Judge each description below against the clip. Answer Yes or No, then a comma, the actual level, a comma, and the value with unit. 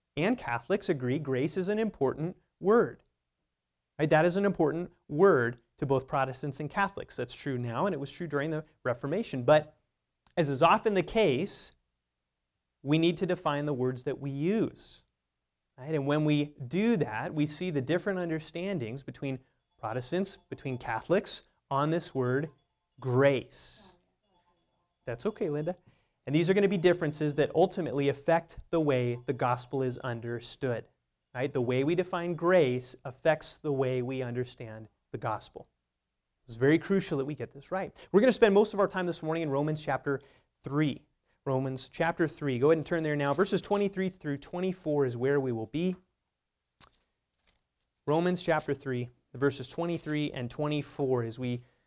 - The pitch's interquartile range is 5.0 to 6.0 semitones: Yes, average, 5.3 semitones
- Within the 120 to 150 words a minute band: No, average, 165 wpm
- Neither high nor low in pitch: Yes, medium, 145 Hz